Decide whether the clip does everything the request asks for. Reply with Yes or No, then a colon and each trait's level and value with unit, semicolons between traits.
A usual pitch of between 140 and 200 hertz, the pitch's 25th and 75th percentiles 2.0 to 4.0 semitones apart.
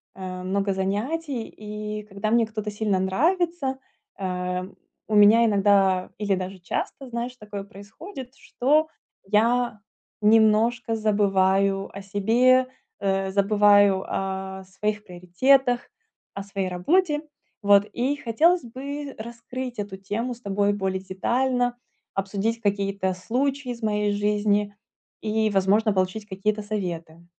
No: high, 210 Hz; average, 3.6 semitones